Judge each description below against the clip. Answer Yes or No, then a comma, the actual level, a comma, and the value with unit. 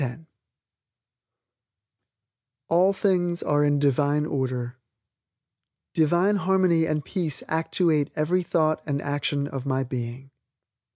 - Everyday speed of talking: No, slow, 100 wpm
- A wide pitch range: No, average, 3.6 semitones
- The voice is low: No, medium, 150 Hz